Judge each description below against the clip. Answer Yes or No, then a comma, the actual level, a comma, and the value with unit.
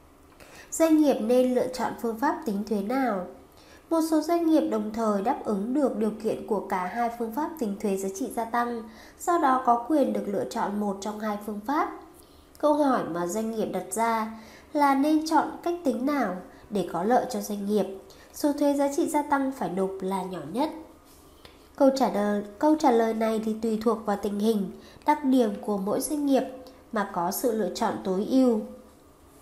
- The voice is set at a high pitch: Yes, high, 235 Hz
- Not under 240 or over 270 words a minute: No, average, 205 wpm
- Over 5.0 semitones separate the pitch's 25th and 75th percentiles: Yes, wide, 5.5 semitones